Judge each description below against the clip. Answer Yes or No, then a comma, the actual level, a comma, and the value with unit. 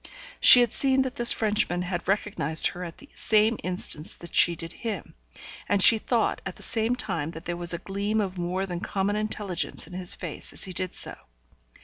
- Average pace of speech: No, fast, 210 wpm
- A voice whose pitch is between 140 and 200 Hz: Yes, high, 190 Hz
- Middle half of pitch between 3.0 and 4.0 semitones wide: Yes, average, 3.7 semitones